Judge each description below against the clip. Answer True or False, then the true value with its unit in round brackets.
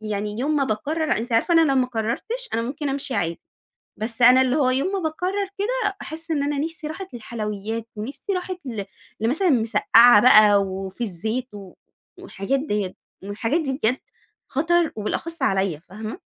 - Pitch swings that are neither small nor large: False (6.6 semitones)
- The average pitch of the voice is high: True (250 Hz)